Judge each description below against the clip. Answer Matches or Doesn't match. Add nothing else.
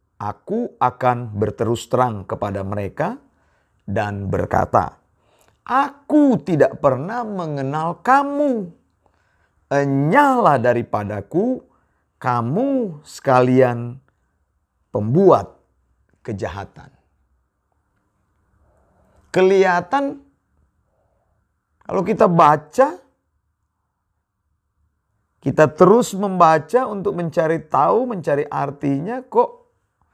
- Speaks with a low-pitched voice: Matches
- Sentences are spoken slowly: Matches